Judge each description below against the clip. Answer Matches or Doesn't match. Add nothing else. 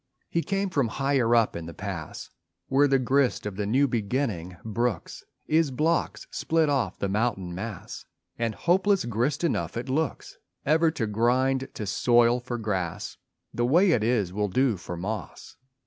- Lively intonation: Doesn't match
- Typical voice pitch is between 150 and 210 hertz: Doesn't match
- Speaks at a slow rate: Doesn't match